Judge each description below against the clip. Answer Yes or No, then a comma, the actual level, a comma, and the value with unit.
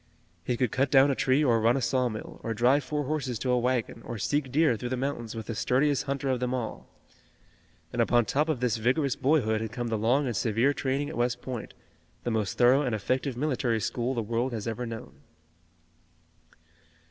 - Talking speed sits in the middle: No, fast, 210 wpm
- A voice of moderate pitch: No, low, 125 Hz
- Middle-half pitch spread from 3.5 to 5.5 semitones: No, average, 2.8 semitones